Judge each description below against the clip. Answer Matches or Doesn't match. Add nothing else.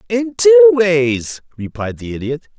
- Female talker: Doesn't match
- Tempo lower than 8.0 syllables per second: Matches